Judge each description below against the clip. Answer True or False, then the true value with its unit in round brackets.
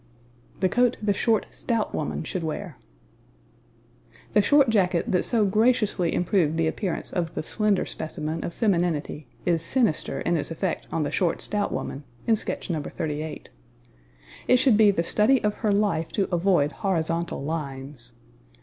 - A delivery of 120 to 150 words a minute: False (160 wpm)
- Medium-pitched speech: True (180 Hz)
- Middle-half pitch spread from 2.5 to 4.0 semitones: False (4.9 semitones)